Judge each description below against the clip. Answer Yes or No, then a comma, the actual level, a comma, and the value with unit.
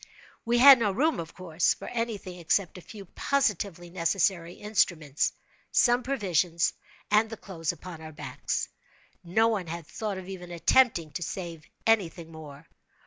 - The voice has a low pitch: No, medium, 185 Hz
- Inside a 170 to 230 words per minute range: No, average, 160 wpm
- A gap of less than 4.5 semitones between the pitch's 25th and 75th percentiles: No, average, 4.8 semitones